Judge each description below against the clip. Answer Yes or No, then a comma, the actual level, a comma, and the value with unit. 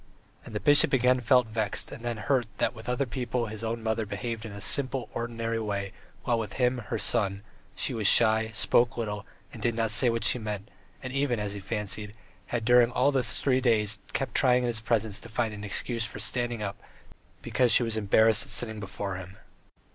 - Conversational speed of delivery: No, fast, 210 wpm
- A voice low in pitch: Yes, low, 115 Hz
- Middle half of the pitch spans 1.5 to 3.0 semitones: Yes, narrow, 2.6 semitones